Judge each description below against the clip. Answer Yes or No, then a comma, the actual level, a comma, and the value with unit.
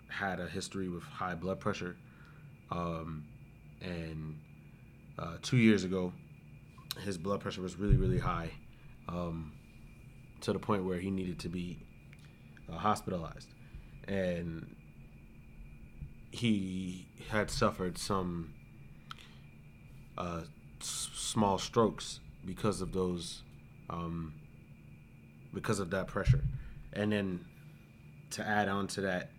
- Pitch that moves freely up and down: No, average, 3.5 semitones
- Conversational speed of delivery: No, slow, 110 wpm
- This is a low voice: Yes, very low, 90 Hz